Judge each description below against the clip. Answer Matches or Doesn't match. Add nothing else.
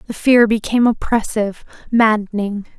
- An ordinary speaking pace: Doesn't match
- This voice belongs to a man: Doesn't match